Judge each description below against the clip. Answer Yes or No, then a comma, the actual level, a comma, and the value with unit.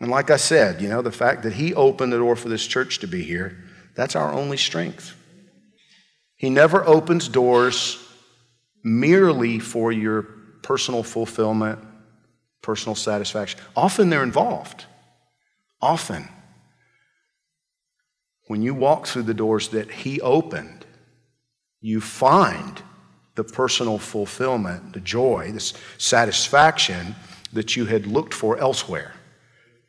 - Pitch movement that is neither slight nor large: No, wide, 5.8 semitones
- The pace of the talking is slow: Yes, slow, 125 wpm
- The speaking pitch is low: Yes, low, 125 Hz